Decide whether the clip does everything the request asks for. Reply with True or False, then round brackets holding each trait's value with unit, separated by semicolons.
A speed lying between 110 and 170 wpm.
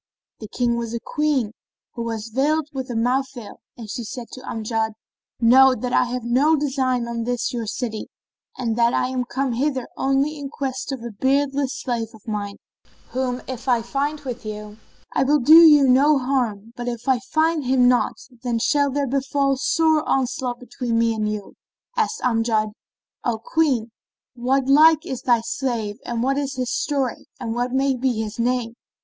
False (185 wpm)